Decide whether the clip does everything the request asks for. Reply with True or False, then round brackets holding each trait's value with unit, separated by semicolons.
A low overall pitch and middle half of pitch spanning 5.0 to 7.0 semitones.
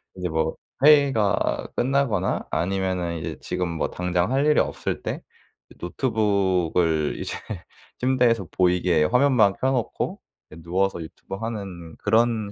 True (95 Hz; 5.3 semitones)